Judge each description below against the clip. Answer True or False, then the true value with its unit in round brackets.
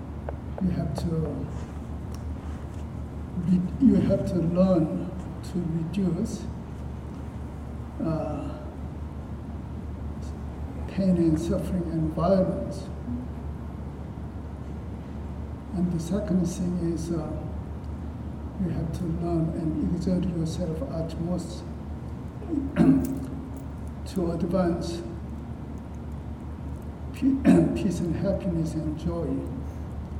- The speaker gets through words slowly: True (75 wpm)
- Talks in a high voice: False (85 Hz)